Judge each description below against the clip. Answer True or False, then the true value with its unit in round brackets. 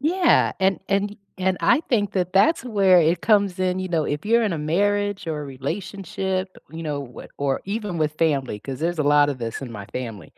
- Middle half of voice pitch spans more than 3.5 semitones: True (5.5 semitones)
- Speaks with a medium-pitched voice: True (180 Hz)